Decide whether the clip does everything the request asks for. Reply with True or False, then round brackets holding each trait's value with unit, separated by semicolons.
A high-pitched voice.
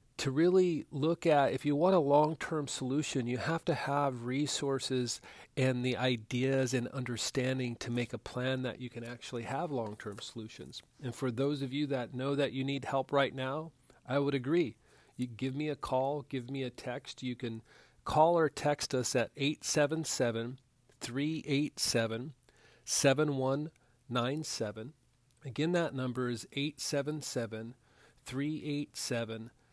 False (130 Hz)